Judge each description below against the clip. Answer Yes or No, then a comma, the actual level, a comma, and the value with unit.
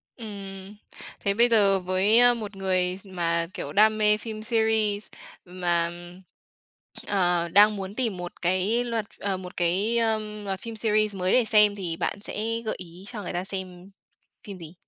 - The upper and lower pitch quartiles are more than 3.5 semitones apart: No, average, 2.9 semitones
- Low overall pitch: No, high, 200 Hz